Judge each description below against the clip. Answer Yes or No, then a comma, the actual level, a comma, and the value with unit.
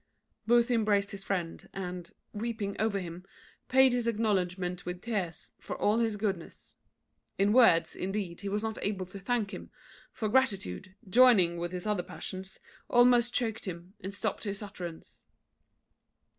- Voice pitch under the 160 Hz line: No, high, 200 Hz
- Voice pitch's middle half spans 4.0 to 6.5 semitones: No, average, 3.6 semitones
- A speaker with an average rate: Yes, average, 150 wpm